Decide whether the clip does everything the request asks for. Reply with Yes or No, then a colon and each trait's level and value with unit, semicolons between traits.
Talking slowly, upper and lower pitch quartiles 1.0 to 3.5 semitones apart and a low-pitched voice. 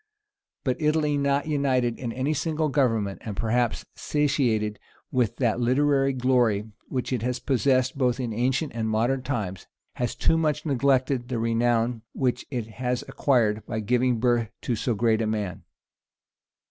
No: average, 155 wpm; average, 3.1 semitones; low, 125 Hz